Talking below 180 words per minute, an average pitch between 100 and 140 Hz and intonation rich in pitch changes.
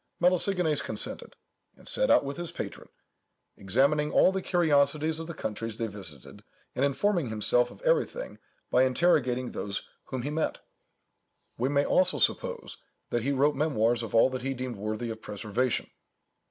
Yes: average, 160 wpm; low, 135 Hz; wide, 5.7 semitones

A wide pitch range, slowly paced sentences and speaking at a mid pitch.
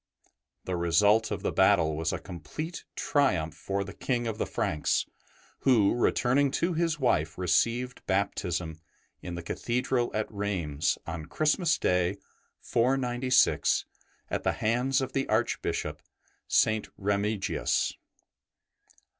No: wide, 6.2 semitones; slow, 125 wpm; low, 105 Hz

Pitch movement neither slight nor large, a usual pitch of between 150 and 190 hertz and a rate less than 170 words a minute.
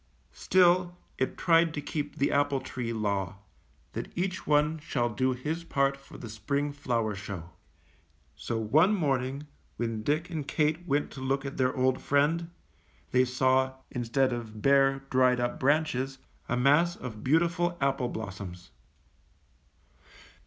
No: average, 3.7 semitones; low, 135 Hz; average, 145 wpm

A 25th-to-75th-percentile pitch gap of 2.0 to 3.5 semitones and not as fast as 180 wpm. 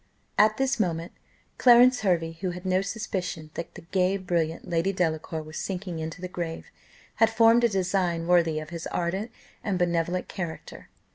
Yes: average, 2.9 semitones; average, 165 wpm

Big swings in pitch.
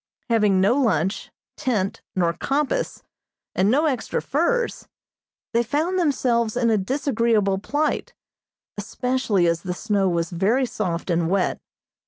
Yes: wide, 5.9 semitones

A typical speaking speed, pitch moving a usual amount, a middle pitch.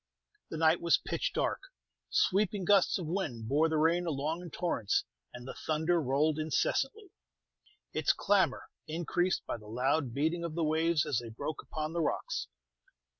Yes: average, 165 wpm; average, 3.2 semitones; medium, 160 Hz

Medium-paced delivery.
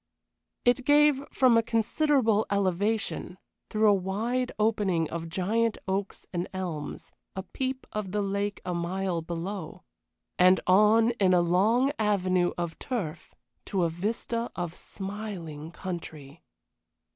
No: slow, 130 wpm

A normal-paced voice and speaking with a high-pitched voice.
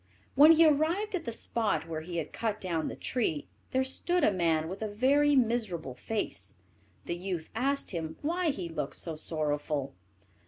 Yes: average, 180 wpm; high, 205 Hz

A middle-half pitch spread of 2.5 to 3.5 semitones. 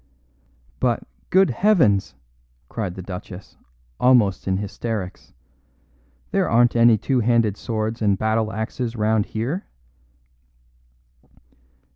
Yes: average, 3.1 semitones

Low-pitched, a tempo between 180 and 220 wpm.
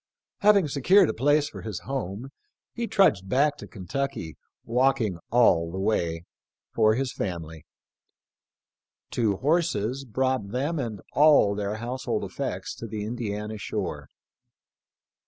No: low, 115 Hz; average, 140 wpm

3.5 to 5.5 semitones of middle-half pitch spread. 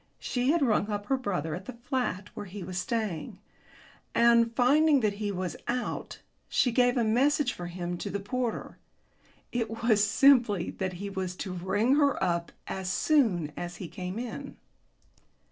Yes: average, 5.2 semitones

